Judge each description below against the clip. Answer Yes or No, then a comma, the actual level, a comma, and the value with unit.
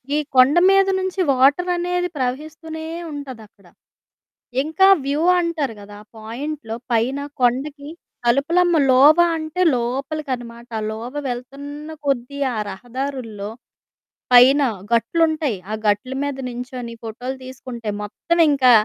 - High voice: Yes, very high, 270 Hz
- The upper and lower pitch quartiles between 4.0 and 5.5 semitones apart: Yes, average, 4.3 semitones